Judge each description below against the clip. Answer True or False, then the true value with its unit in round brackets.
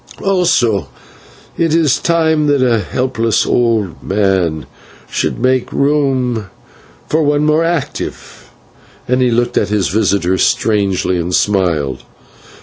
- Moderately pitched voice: False (120 Hz)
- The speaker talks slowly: True (125 wpm)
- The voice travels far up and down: True (6.8 semitones)